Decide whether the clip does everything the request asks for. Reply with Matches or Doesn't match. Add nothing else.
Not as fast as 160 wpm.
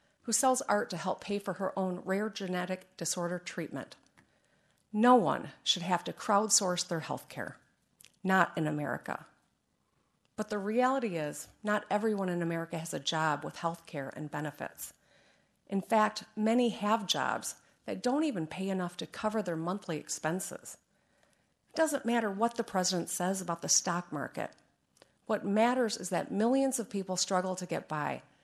Doesn't match